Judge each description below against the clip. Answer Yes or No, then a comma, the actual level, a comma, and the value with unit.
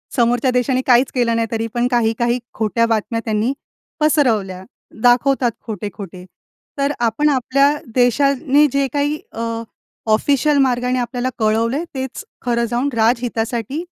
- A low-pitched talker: No, high, 245 Hz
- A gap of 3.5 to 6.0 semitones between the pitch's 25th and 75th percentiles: No, average, 3.0 semitones